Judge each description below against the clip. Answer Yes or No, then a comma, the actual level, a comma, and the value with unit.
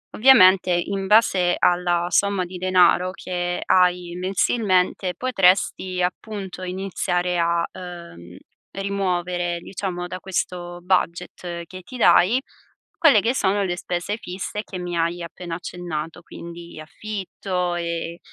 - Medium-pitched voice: Yes, medium, 180 Hz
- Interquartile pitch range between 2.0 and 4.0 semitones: No, narrow, 1.6 semitones